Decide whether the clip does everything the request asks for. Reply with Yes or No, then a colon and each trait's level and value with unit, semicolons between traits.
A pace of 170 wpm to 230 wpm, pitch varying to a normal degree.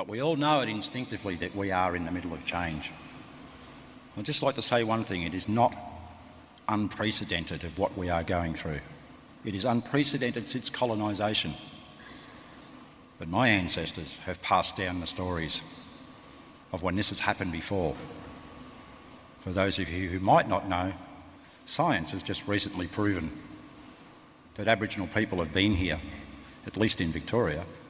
No: average, 155 wpm; average, 3.3 semitones